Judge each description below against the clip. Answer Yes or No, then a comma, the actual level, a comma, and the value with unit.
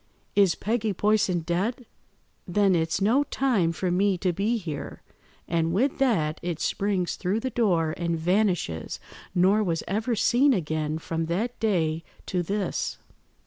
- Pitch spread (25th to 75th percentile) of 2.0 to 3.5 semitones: No, average, 4.5 semitones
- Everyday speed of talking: Yes, average, 145 wpm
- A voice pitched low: No, medium, 185 Hz